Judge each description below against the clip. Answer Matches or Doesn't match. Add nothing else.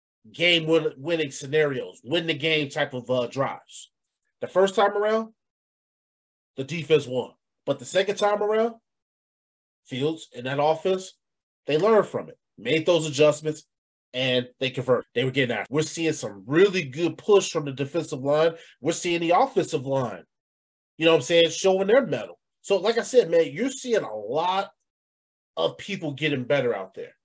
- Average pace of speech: Matches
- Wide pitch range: Matches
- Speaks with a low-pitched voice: Doesn't match